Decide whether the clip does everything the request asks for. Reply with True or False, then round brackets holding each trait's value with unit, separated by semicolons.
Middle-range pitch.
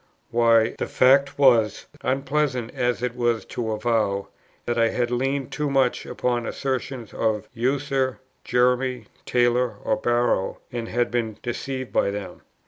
False (120 Hz)